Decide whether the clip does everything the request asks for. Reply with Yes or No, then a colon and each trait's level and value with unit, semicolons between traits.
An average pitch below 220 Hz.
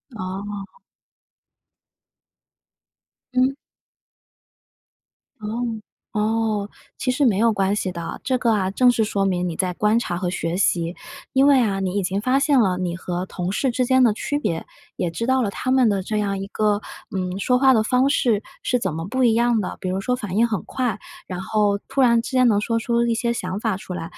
Yes: high, 210 Hz